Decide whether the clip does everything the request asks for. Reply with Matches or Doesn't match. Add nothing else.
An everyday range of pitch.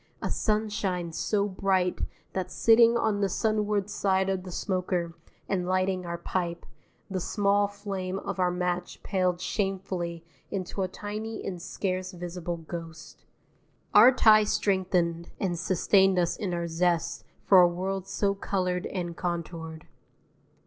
Doesn't match